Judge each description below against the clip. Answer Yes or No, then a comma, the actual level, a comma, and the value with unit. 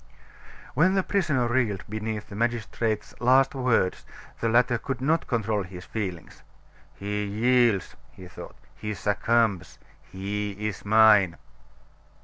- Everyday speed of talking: No, slow, 125 wpm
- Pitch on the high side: No, low, 110 Hz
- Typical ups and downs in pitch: Yes, average, 3.3 semitones